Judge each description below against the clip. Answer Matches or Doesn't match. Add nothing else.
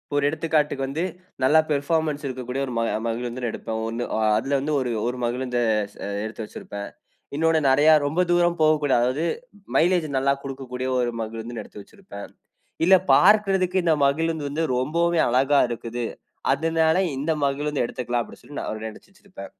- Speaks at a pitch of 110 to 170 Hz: Matches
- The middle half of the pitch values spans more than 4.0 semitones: Matches